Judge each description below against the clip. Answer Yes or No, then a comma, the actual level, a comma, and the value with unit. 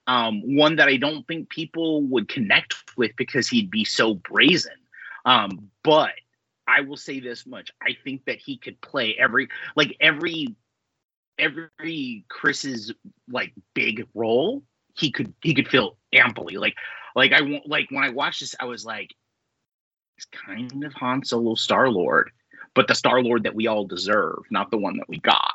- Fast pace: No, average, 175 wpm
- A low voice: No, medium, 145 Hz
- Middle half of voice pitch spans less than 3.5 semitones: No, average, 5.3 semitones